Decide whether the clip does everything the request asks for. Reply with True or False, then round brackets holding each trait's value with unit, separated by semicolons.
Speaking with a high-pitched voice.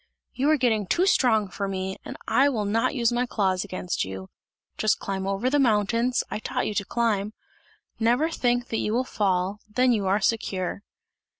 True (215 Hz)